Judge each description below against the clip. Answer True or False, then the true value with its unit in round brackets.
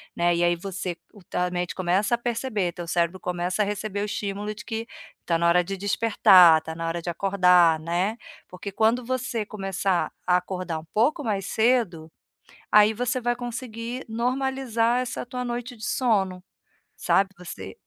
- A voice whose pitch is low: False (200 Hz)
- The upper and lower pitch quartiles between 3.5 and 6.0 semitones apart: True (4.7 semitones)